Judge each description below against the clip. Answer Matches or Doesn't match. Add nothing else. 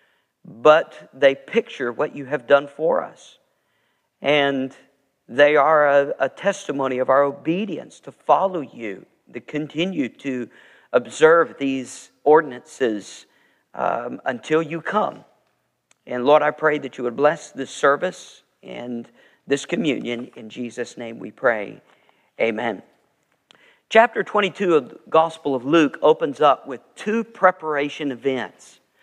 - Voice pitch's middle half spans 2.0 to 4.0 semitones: Matches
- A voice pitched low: Doesn't match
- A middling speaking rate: Doesn't match